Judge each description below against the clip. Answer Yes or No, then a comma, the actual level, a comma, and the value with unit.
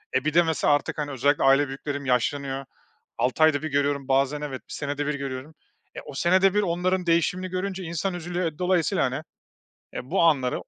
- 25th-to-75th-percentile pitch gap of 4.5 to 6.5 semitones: No, average, 4.0 semitones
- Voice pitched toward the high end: No, medium, 150 Hz